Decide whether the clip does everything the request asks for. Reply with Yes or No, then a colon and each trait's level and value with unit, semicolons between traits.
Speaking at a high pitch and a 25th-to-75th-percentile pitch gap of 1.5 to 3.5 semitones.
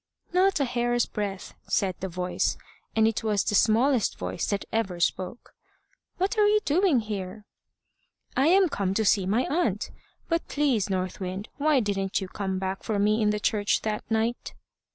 No: high, 215 Hz; average, 4.6 semitones